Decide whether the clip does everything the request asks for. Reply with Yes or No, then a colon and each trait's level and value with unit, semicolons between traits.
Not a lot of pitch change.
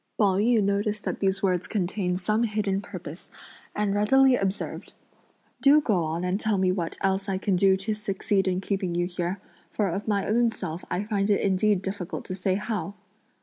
Yes: narrow, 2.2 semitones